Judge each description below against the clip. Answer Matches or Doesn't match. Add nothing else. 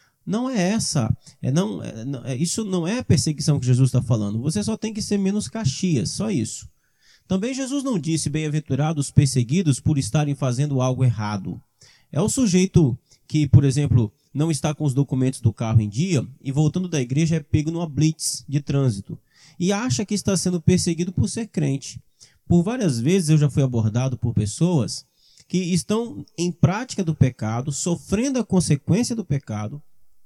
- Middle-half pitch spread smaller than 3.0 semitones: Doesn't match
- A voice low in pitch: Doesn't match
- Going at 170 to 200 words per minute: Matches